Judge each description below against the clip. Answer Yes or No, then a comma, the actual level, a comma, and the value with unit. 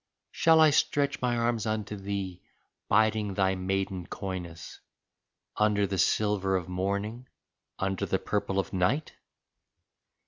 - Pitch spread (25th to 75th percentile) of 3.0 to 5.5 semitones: No, narrow, 2.5 semitones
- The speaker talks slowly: Yes, slow, 125 wpm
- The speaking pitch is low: Yes, low, 100 Hz